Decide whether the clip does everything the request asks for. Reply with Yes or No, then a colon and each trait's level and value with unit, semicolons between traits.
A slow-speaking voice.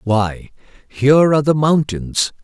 Yes: slow, 125 wpm